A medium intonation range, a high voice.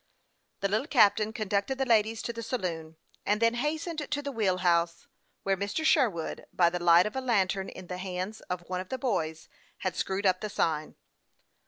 Yes: average, 4.3 semitones; high, 200 Hz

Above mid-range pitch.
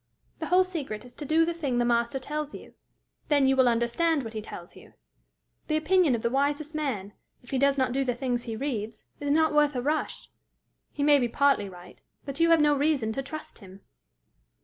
Yes: very high, 275 Hz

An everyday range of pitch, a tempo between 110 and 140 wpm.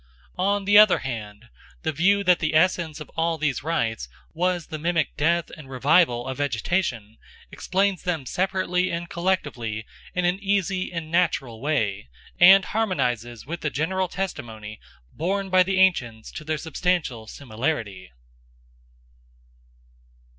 No: wide, 6.8 semitones; slow, 135 wpm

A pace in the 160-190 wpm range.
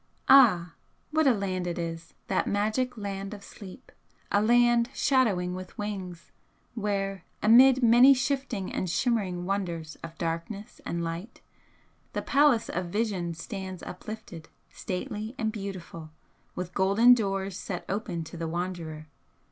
No: slow, 135 wpm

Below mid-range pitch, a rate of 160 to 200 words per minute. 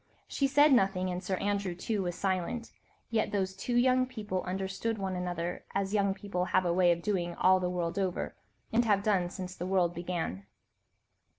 No: high, 190 Hz; average, 190 wpm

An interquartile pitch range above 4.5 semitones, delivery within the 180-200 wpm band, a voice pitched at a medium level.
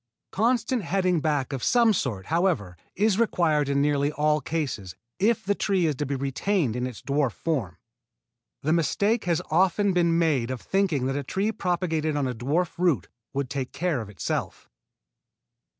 No: average, 5.3 semitones; average, 170 wpm; medium, 155 Hz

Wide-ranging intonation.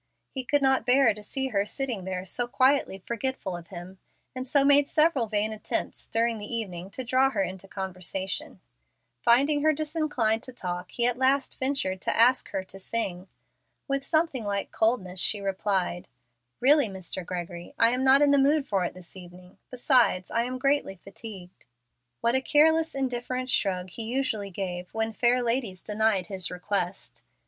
Yes: wide, 5.7 semitones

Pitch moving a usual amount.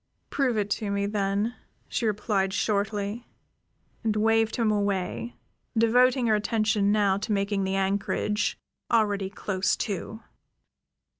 No: narrow, 1.9 semitones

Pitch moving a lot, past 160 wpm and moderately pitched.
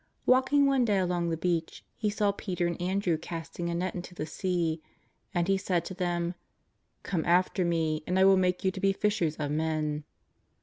No: narrow, 2.5 semitones; fast, 205 wpm; medium, 180 Hz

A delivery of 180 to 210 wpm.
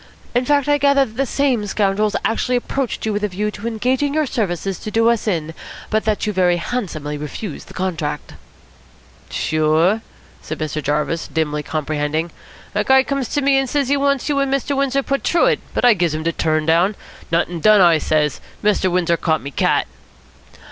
Yes: average, 195 wpm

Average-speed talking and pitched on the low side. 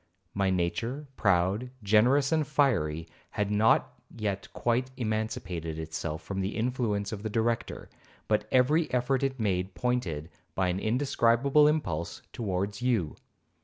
No: slow, 130 wpm; low, 110 Hz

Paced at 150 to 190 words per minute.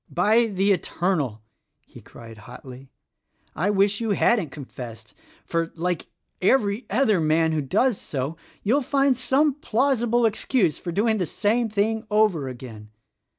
No: average, 140 wpm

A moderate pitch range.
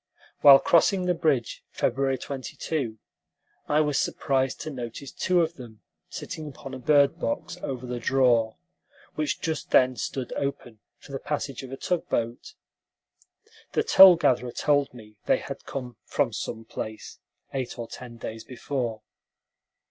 Yes: average, 3.8 semitones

